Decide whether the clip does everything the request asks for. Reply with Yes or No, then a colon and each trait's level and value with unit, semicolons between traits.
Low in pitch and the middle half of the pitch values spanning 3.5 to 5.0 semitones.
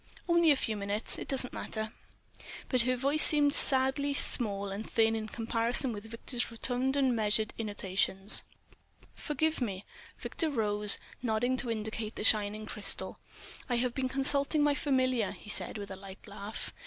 No: high, 230 Hz; average, 4.0 semitones